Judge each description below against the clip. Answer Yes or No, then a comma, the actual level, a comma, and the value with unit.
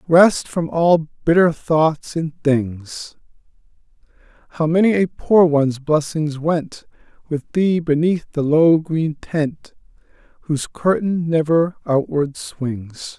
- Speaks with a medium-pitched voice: Yes, medium, 155 Hz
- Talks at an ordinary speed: No, slow, 120 wpm